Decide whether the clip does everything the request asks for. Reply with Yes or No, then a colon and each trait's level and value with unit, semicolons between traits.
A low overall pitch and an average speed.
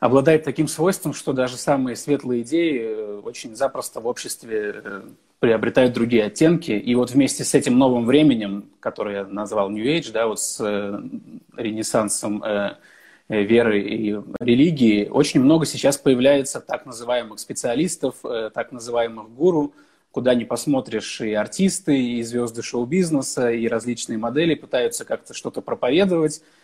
Yes: low, 125 Hz; average, 135 wpm